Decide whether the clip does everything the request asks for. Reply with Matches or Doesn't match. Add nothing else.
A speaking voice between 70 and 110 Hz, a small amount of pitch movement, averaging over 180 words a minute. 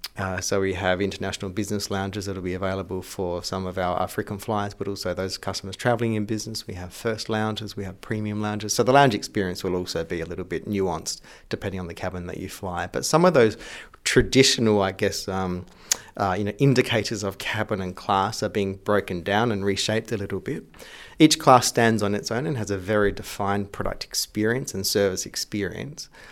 Matches